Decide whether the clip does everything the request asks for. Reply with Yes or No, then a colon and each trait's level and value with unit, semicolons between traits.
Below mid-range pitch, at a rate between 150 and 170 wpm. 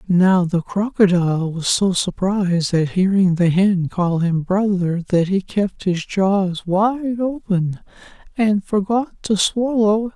No: high, 195 Hz; average, 155 wpm